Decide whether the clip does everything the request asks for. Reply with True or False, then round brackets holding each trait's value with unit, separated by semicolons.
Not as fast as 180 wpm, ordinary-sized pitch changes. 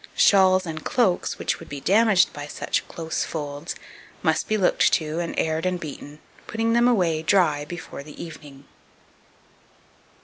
True (150 wpm; 3.8 semitones)